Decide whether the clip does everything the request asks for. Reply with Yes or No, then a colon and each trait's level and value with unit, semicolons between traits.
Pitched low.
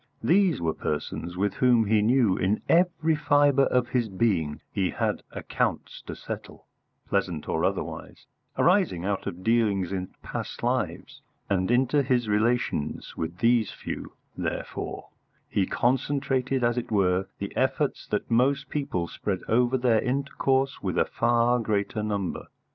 Yes: low, 115 Hz